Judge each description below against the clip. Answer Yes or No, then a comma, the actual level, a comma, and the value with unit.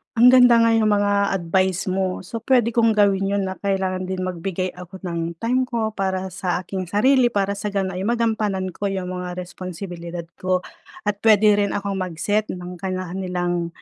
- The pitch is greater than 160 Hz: Yes, high, 190 Hz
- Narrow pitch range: Yes, narrow, 2.3 semitones